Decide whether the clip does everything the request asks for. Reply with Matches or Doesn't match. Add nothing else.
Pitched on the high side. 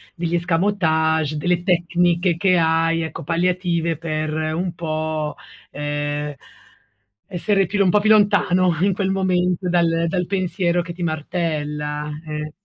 Doesn't match